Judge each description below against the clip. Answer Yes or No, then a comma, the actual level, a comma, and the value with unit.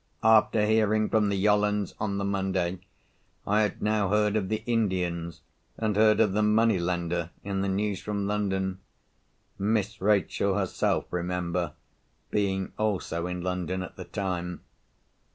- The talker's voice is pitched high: No, low, 100 Hz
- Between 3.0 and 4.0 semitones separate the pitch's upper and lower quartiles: No, narrow, 2.6 semitones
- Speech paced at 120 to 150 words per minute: Yes, average, 140 wpm